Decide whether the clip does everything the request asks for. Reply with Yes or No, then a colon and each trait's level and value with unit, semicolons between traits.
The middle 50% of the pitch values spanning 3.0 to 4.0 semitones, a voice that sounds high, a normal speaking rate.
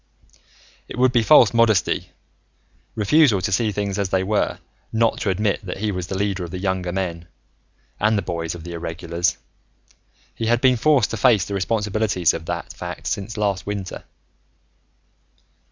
No: average, 3.4 semitones; low, 100 Hz; average, 170 wpm